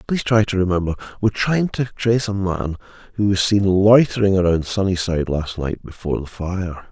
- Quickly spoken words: No, average, 190 wpm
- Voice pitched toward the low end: Yes, very low, 95 Hz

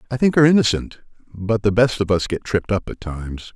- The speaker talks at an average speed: No, fast, 235 wpm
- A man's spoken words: Yes, male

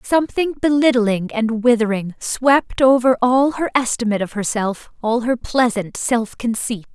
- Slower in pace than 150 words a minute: Yes, average, 140 wpm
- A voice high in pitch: Yes, high, 235 Hz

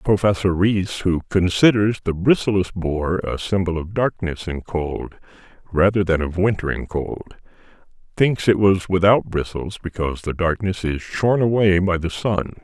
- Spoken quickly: No, average, 155 wpm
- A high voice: No, very low, 95 Hz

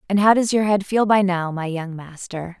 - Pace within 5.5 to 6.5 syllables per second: No, 5.0 syllables/s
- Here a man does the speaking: No, female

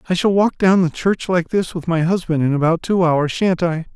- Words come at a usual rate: No, fast, 260 wpm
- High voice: No, medium, 175 Hz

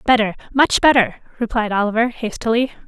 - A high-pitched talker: Yes, high, 235 Hz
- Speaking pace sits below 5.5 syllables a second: No, 5.9 syllables/s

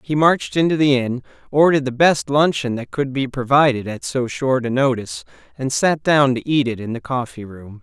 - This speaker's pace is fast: Yes, fast, 215 wpm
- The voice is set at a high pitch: No, low, 130 Hz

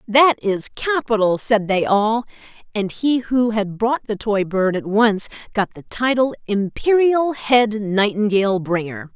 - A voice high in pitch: Yes, high, 215 Hz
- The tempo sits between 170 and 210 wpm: No, average, 150 wpm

